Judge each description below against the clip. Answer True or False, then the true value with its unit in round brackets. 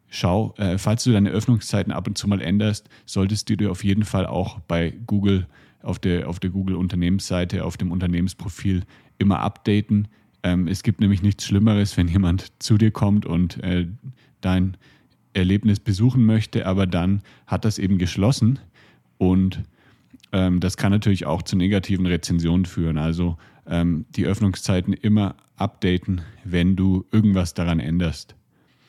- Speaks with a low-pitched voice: True (95 Hz)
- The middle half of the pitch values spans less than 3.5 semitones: True (2.8 semitones)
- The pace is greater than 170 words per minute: False (155 wpm)